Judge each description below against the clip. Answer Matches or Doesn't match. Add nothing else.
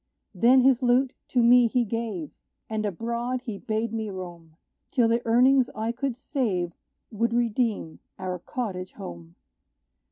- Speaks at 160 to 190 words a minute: Doesn't match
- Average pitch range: Matches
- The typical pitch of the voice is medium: Doesn't match